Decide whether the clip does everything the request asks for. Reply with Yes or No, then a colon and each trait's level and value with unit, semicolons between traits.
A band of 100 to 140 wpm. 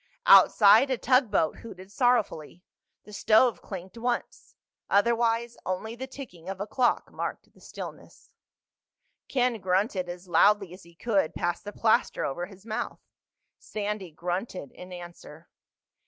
Yes: slow, 135 wpm